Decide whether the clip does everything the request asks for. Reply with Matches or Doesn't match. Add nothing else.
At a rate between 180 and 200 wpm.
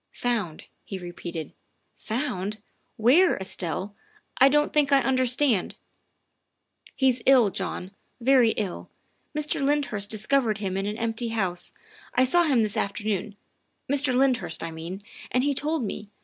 Doesn't match